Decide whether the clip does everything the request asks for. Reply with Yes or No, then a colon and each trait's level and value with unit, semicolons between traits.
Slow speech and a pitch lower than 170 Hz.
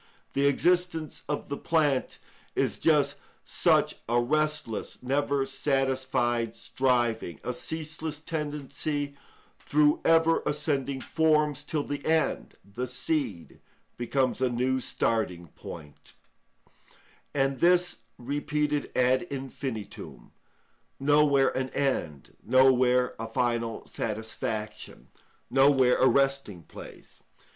Yes: slow, 100 wpm; low, 135 Hz